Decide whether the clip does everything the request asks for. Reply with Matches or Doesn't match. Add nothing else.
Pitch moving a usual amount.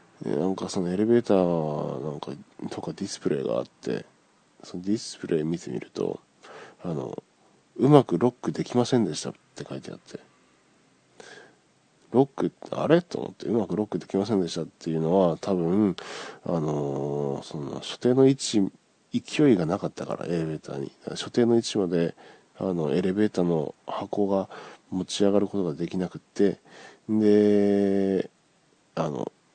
Matches